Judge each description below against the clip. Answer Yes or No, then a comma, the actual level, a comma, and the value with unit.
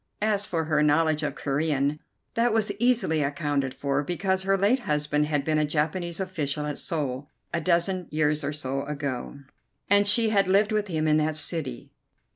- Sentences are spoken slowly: No, average, 180 wpm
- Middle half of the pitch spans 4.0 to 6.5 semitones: Yes, average, 4.4 semitones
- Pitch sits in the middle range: Yes, medium, 155 Hz